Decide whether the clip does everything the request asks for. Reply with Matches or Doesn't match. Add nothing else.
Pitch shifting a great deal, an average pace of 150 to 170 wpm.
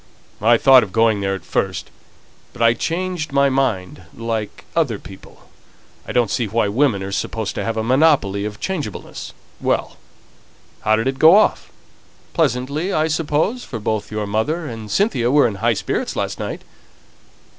Matches